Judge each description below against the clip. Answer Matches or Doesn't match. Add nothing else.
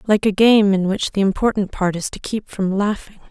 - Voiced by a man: Doesn't match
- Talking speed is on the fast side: Matches